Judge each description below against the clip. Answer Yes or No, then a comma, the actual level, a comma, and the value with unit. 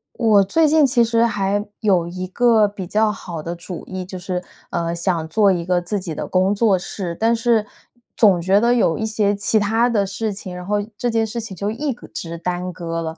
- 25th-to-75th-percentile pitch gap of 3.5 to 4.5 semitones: Yes, average, 3.8 semitones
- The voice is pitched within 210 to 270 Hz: No, high, 200 Hz